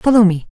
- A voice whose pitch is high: Yes, high, 205 Hz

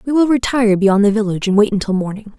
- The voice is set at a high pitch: Yes, high, 215 Hz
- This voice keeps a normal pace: No, fast, 250 wpm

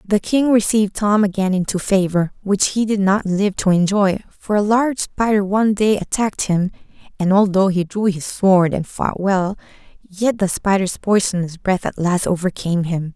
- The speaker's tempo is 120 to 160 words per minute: No, average, 185 wpm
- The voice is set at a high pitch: Yes, high, 195 Hz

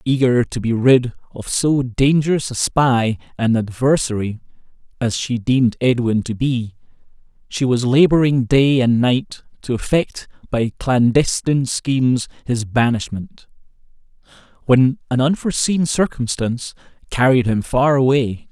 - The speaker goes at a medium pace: No, slow, 125 wpm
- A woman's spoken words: No, male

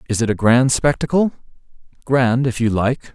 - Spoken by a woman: No, male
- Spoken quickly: No, average, 170 wpm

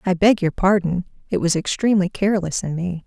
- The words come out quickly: No, average, 195 wpm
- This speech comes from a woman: Yes, female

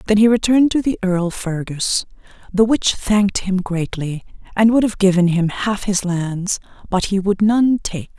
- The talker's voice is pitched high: Yes, high, 200 Hz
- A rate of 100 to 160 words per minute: No, average, 185 wpm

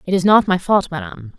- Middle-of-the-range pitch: Yes, medium, 180 Hz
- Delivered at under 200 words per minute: No, fast, 260 wpm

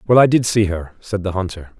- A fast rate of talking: Yes, fast, 270 wpm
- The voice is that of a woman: No, male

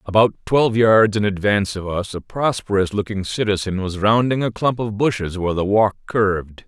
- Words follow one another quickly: No, average, 190 wpm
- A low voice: Yes, low, 105 Hz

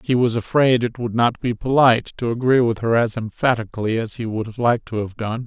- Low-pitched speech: Yes, low, 115 Hz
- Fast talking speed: Yes, fast, 230 wpm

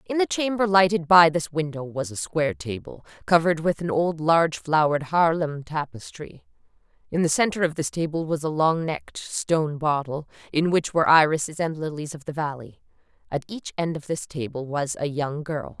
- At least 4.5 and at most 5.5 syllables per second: Yes, 5.3 syllables/s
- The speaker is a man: No, female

